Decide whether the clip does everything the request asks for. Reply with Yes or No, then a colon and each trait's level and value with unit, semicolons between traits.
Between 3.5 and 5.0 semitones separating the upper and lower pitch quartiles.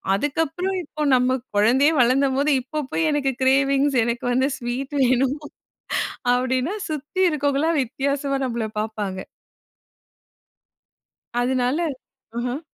No: average, 2.7 semitones